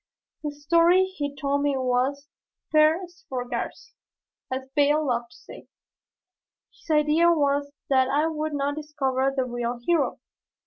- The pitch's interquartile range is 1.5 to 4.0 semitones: Yes, average, 2.7 semitones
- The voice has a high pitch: Yes, very high, 285 Hz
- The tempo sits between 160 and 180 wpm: No, slow, 135 wpm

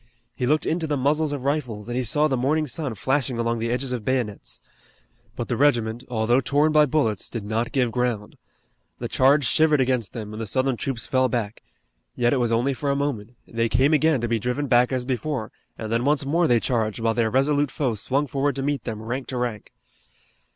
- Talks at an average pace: No, fast, 220 wpm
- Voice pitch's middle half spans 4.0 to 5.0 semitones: No, average, 3.5 semitones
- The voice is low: Yes, low, 125 Hz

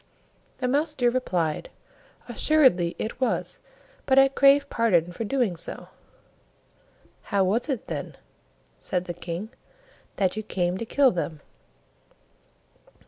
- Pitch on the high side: Yes, high, 220 Hz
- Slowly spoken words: Yes, slow, 125 wpm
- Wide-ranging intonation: Yes, wide, 7.0 semitones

